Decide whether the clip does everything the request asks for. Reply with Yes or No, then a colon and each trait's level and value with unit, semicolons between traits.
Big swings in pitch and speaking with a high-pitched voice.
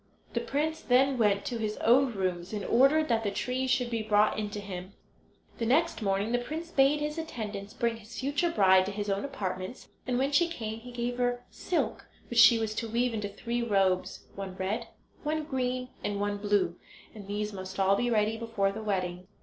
No: average, 3.9 semitones; high, 225 Hz